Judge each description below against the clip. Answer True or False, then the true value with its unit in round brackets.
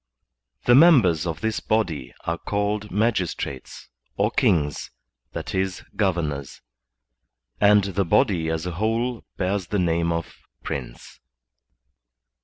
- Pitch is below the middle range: True (95 Hz)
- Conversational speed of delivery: False (115 wpm)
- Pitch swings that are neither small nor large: True (4.2 semitones)